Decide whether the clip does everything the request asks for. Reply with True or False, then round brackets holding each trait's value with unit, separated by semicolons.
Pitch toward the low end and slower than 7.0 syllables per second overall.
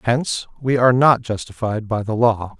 True (115 Hz; 5.2 syllables/s)